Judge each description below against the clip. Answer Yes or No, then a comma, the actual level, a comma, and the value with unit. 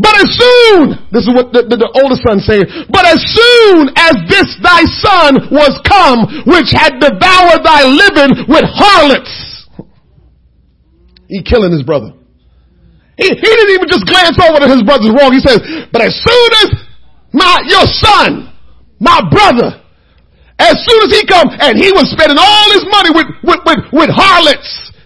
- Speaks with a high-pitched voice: Yes, very high, 320 Hz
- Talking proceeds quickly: No, average, 170 wpm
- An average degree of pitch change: No, wide, 6.7 semitones